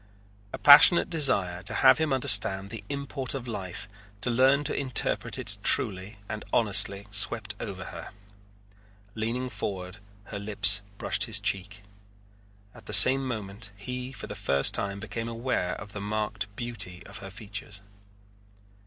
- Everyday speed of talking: Yes, average, 150 wpm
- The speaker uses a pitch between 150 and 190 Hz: No, low, 105 Hz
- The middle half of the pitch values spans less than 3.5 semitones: No, average, 4.2 semitones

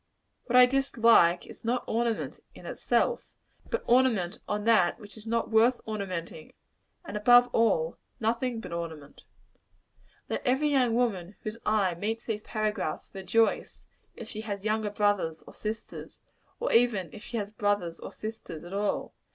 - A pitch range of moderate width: Yes, average, 3.0 semitones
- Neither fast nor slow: Yes, average, 155 wpm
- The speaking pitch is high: Yes, high, 215 Hz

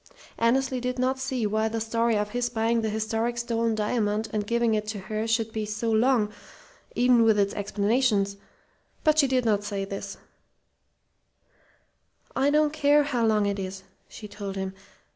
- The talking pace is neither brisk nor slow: Yes, average, 175 wpm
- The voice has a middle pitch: No, high, 225 Hz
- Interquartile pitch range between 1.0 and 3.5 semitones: Yes, average, 2.7 semitones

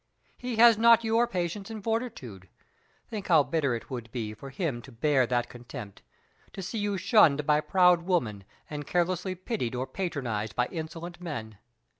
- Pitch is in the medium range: Yes, medium, 160 Hz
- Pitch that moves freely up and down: Yes, wide, 7.9 semitones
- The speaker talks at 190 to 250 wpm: No, average, 170 wpm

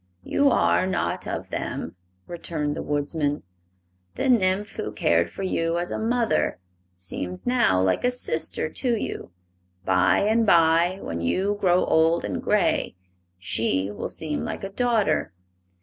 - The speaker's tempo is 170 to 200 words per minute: No, average, 150 wpm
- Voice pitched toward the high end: No, medium, 170 Hz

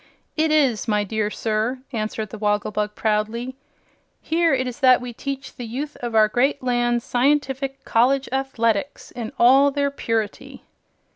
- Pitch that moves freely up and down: No, average, 3.7 semitones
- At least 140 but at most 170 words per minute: Yes, average, 150 wpm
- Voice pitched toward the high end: Yes, high, 245 Hz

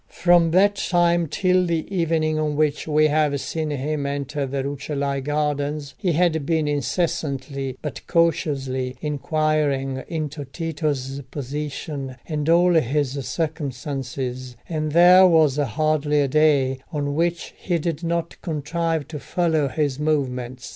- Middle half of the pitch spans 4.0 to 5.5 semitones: No, average, 2.8 semitones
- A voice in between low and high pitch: Yes, medium, 150 Hz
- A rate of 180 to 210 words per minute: No, slow, 135 wpm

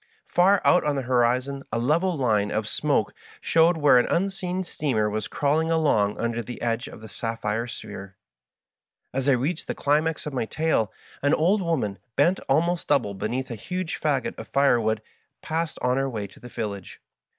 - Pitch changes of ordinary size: No, wide, 6.1 semitones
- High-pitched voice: No, low, 135 Hz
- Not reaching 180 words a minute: No, average, 185 wpm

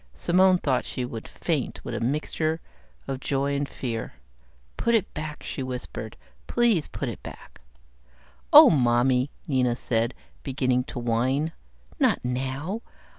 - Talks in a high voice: No, low, 135 Hz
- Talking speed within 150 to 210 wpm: No, slow, 135 wpm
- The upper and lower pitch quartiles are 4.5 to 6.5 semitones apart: No, average, 3.7 semitones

